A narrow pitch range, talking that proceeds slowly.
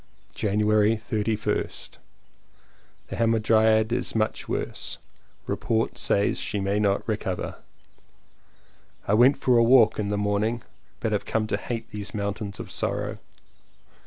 Yes: narrow, 1.6 semitones; slow, 120 wpm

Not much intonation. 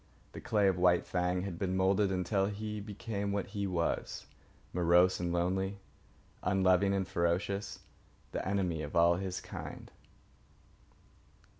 Yes: narrow, 2.0 semitones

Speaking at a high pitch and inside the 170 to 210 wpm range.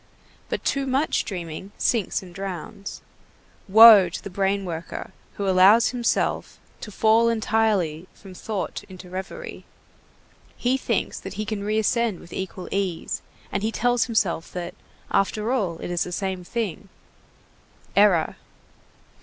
No: high, 200 Hz; average, 140 wpm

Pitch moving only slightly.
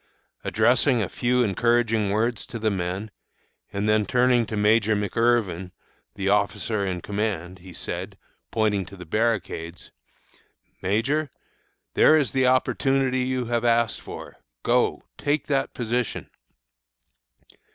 No: average, 3.6 semitones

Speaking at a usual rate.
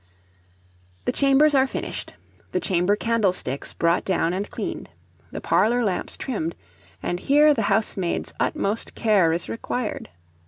No: slow, 130 wpm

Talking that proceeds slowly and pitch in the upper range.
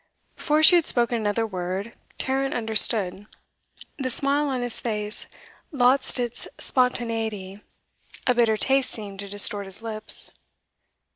Yes: slow, 130 wpm; high, 230 Hz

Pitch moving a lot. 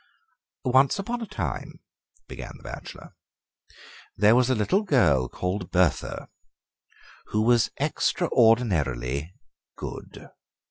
Yes: wide, 7.8 semitones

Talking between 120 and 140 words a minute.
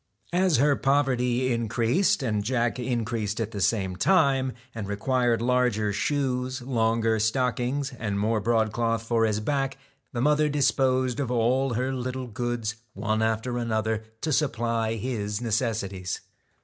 Yes: slow, 135 wpm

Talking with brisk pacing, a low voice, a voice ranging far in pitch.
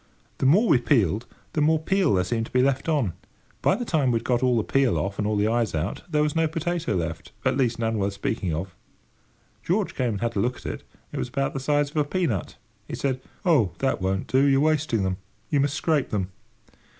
Yes: fast, 235 wpm; low, 130 Hz; wide, 6.1 semitones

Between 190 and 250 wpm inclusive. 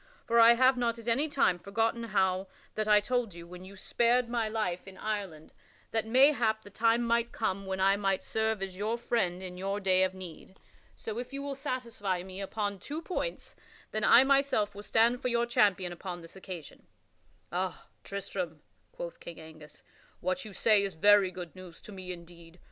Yes: average, 195 wpm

